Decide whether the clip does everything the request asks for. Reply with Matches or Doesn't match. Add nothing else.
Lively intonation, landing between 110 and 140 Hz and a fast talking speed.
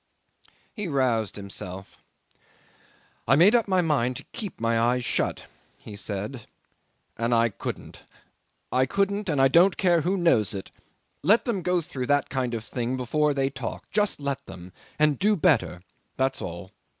Doesn't match